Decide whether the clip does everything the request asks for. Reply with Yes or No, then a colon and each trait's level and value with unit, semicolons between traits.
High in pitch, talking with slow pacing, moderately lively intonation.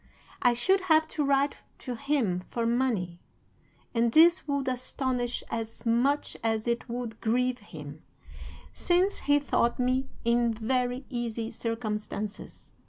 Yes: high, 245 Hz; slow, 130 wpm; average, 3.2 semitones